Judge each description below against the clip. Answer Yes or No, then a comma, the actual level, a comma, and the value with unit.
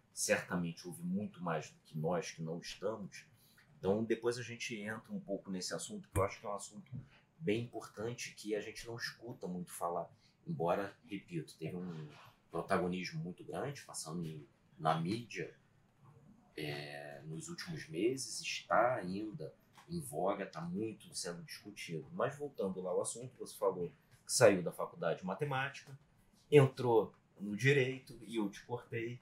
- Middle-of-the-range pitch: No, low, 120 Hz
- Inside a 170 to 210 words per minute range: No, average, 160 wpm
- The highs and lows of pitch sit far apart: Yes, wide, 7.4 semitones